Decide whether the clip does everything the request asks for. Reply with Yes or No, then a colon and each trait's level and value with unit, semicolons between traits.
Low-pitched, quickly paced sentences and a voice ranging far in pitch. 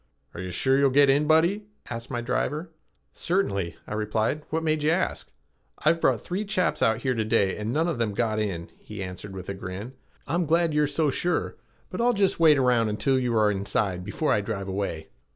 Yes: low, 125 Hz; fast, 210 wpm; wide, 7.2 semitones